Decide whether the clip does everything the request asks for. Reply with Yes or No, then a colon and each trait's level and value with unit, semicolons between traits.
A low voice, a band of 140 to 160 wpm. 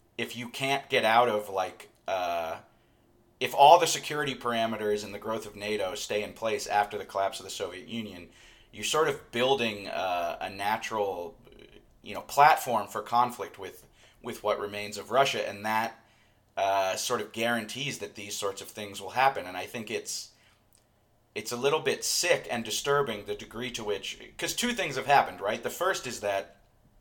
No: low, 110 Hz; average, 185 wpm